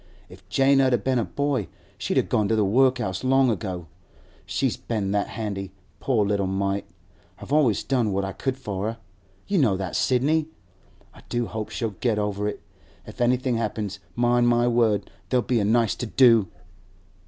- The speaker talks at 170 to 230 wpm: Yes, average, 180 wpm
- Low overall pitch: Yes, low, 115 Hz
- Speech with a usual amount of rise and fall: Yes, average, 3.9 semitones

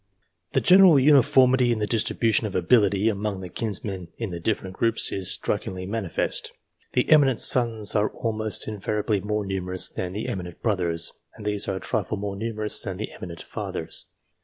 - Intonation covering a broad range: No, average, 3.2 semitones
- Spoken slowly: No, average, 170 wpm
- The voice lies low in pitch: Yes, low, 105 Hz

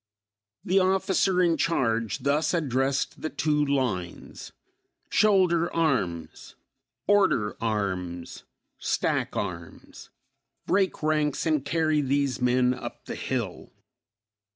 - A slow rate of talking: Yes, slow, 100 wpm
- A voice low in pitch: No, medium, 145 Hz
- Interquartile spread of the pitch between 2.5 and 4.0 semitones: No, wide, 5.6 semitones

